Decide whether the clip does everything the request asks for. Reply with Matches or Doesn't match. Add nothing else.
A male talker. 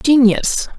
Doesn't match